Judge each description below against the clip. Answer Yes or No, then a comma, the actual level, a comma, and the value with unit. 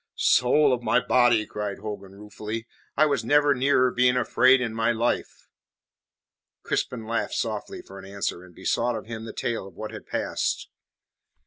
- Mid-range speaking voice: No, low, 115 Hz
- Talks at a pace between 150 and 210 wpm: Yes, average, 160 wpm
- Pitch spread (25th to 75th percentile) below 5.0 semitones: Yes, average, 3.0 semitones